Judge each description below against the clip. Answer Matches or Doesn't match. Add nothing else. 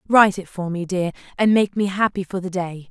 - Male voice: Doesn't match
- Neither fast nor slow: Doesn't match